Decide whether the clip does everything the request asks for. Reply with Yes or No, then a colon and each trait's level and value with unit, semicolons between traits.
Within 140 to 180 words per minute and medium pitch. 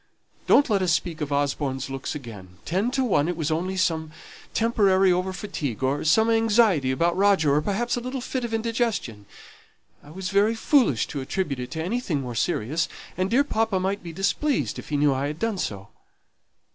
No: average, 195 wpm; medium, 180 Hz